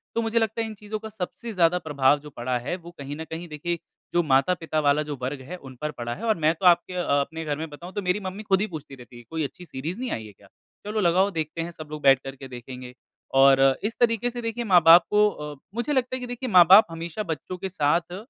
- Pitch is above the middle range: No, medium, 170 Hz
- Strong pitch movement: Yes, wide, 6.3 semitones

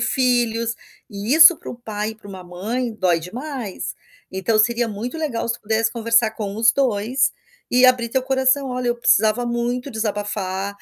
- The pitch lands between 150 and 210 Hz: No, high, 230 Hz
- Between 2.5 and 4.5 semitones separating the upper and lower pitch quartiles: Yes, average, 3.2 semitones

